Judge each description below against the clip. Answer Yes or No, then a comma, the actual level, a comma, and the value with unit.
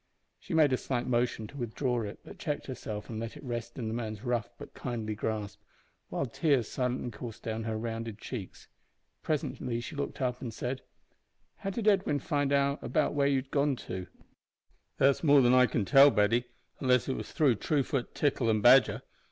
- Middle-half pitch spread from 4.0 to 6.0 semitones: No, average, 3.6 semitones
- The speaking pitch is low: Yes, low, 125 Hz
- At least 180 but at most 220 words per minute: Yes, average, 190 wpm